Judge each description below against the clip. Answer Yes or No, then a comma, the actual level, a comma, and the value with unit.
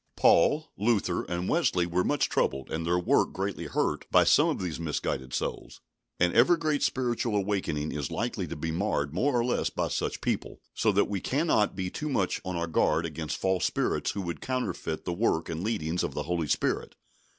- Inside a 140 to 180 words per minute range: No, average, 200 wpm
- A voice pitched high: No, very low, 90 Hz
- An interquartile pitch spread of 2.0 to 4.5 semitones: No, average, 5.2 semitones